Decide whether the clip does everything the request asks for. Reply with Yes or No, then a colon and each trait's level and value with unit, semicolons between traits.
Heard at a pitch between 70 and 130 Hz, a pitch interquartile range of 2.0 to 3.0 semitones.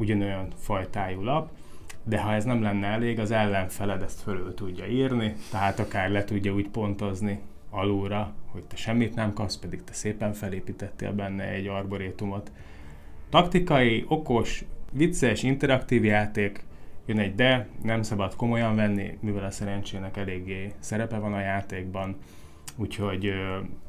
Yes: low, 100 Hz; narrow, 2.4 semitones